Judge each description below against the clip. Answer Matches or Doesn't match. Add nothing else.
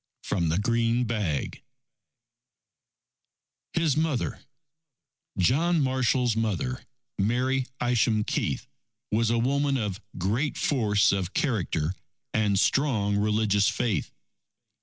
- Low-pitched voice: Matches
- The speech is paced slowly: Matches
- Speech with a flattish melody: Doesn't match